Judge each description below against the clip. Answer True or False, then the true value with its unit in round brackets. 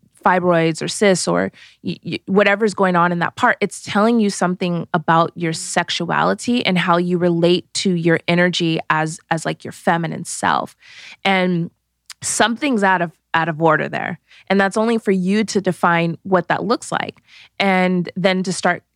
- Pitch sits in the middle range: True (180 Hz)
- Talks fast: False (175 wpm)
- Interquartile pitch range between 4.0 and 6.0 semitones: False (2.7 semitones)